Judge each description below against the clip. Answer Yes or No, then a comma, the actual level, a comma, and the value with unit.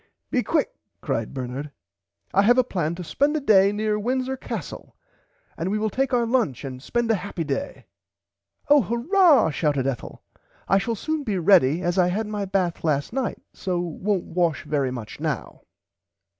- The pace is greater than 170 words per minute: Yes, average, 185 wpm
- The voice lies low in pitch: No, high, 195 Hz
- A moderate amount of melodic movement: No, wide, 6.8 semitones